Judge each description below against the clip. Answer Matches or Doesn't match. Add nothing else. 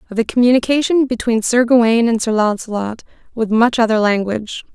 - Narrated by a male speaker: Doesn't match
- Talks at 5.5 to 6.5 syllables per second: Matches